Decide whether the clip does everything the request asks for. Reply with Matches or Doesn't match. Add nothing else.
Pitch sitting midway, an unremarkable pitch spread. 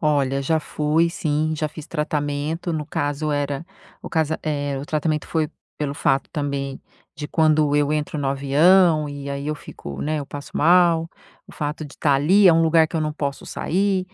Doesn't match